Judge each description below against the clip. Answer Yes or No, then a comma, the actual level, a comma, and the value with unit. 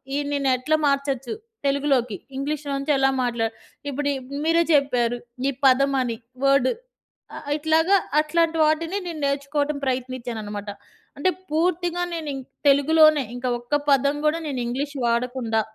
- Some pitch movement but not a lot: Yes, average, 3.3 semitones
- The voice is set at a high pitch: Yes, very high, 280 Hz